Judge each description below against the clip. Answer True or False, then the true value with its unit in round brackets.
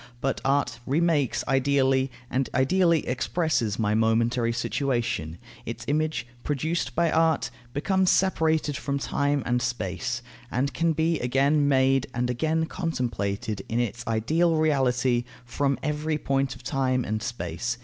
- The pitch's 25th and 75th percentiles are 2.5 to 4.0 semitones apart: False (4.4 semitones)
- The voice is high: False (135 Hz)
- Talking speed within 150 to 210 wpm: False (135 wpm)